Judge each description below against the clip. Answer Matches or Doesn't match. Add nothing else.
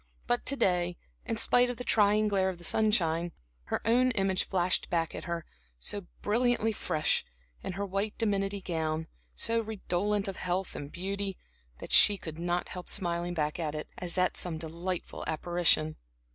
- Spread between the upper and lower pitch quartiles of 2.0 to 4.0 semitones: Matches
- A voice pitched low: Doesn't match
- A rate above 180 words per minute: Doesn't match